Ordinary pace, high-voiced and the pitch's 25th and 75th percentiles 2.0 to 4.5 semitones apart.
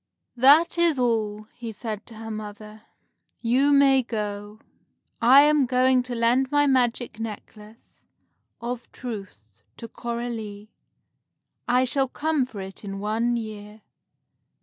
No: slow, 125 wpm; high, 235 Hz; average, 3.3 semitones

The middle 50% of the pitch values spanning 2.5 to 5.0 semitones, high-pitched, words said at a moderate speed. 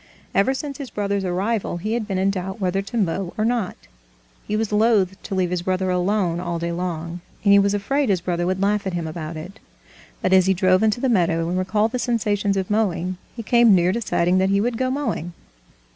No: average, 3.1 semitones; high, 195 Hz; fast, 225 wpm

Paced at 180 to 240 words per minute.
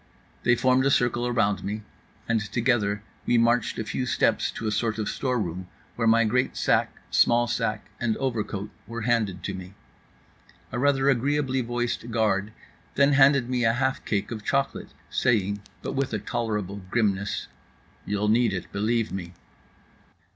No: average, 160 wpm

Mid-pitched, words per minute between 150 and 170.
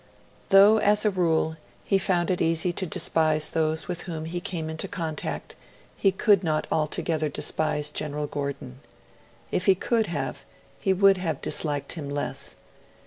Yes: medium, 165 Hz; average, 155 wpm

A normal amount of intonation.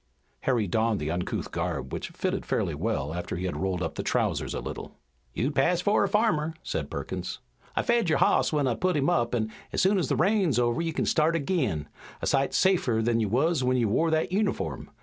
No: wide, 7.5 semitones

